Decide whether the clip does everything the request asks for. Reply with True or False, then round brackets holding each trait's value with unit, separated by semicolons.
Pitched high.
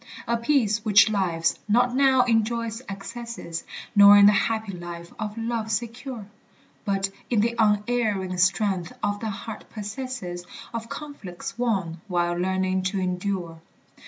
True (210 Hz)